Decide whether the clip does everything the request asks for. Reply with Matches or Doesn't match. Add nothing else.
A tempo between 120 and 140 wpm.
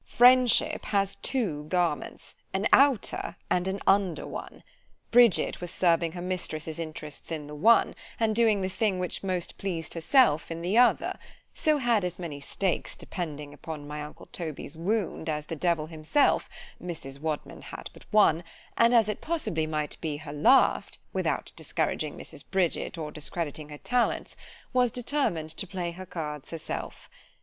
Doesn't match